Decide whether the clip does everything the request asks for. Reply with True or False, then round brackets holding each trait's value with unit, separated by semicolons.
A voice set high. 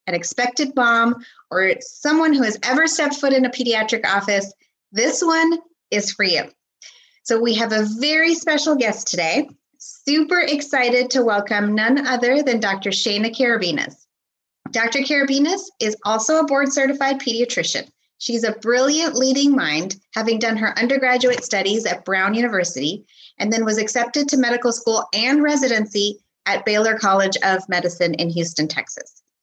True (235 Hz)